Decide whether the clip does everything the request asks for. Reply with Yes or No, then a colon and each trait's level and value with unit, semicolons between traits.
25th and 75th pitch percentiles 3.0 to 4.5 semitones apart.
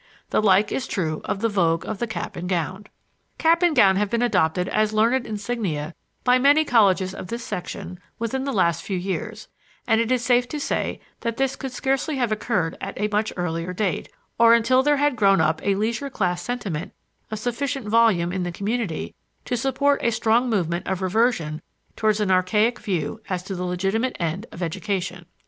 No: average, 4.9 semitones